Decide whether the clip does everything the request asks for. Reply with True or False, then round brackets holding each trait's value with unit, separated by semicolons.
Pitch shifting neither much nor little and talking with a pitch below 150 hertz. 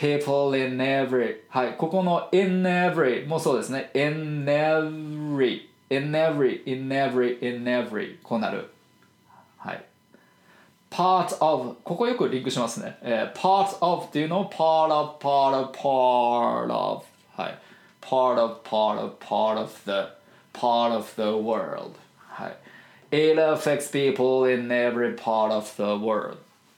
True (4.3 semitones; 135 Hz)